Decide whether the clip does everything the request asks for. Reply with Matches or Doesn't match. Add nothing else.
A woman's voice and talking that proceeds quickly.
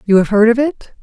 Matches